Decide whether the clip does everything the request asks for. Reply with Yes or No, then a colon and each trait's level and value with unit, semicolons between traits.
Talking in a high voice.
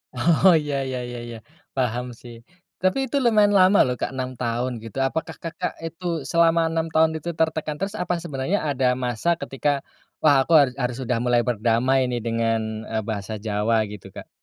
No: low, 135 Hz